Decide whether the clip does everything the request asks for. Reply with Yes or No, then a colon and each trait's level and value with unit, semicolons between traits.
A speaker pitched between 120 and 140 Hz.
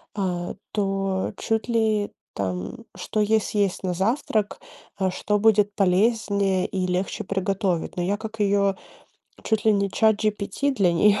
No: high, 200 Hz